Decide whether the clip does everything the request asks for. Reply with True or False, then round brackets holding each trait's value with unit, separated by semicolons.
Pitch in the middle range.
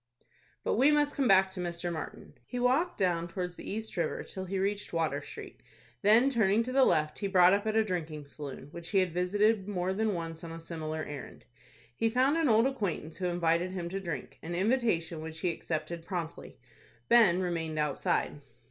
True (180 Hz)